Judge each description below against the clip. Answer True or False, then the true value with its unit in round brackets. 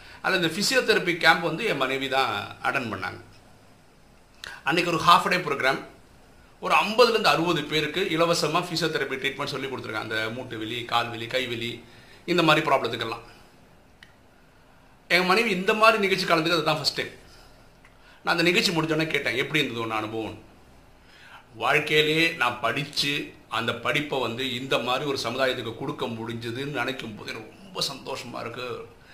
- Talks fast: True (135 wpm)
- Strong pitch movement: True (5.7 semitones)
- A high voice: False (135 Hz)